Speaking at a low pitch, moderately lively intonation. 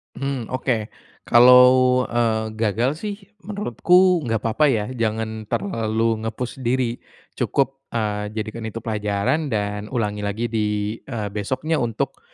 Yes: low, 115 Hz; average, 3.1 semitones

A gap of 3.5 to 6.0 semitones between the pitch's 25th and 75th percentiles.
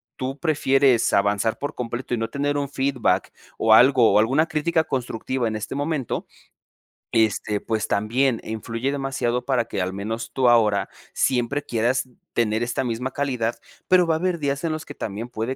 Yes: average, 3.9 semitones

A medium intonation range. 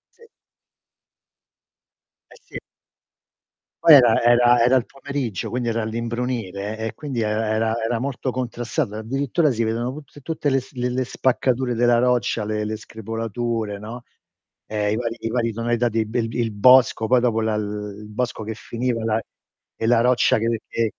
No: narrow, 2.1 semitones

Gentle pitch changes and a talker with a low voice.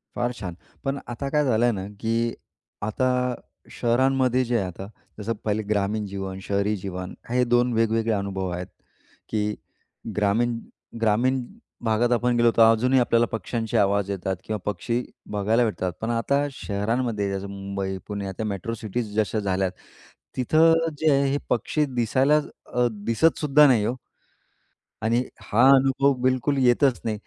No: average, 3.6 semitones; low, 115 Hz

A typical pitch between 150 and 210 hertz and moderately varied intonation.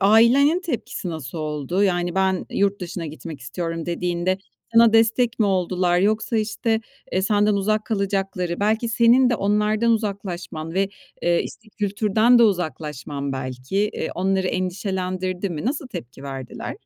Yes: high, 190 Hz; average, 3.9 semitones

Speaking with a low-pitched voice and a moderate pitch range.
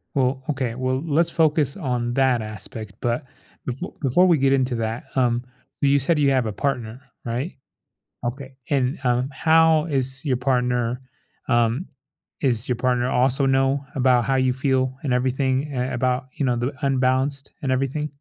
No: low, 130 Hz; narrow, 2.0 semitones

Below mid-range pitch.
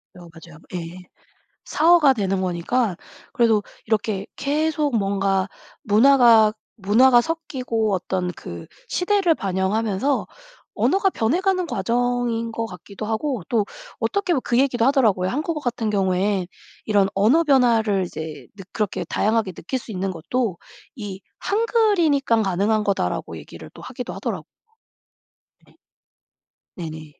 No: high, 220 Hz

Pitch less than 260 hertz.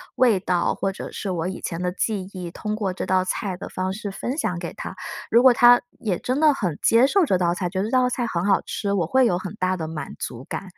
Yes: high, 190 Hz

